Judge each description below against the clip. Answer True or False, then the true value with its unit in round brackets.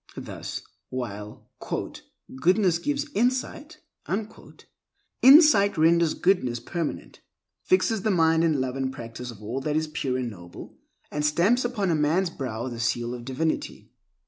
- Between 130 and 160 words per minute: True (140 wpm)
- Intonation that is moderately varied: False (7.6 semitones)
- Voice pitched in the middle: True (155 Hz)